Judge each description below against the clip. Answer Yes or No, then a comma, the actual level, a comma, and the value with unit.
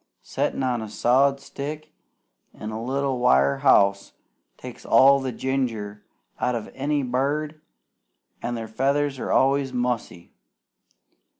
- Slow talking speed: Yes, slow, 125 wpm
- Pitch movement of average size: Yes, average, 3.5 semitones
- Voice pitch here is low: Yes, low, 130 Hz